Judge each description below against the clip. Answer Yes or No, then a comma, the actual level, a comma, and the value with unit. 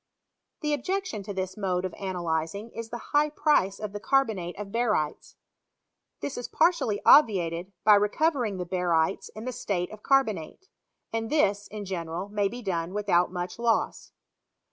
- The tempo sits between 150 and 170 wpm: Yes, average, 160 wpm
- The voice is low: No, high, 205 Hz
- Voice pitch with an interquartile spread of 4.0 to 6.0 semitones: Yes, average, 4.7 semitones